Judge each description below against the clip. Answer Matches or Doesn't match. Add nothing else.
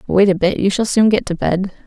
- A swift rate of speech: Matches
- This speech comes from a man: Doesn't match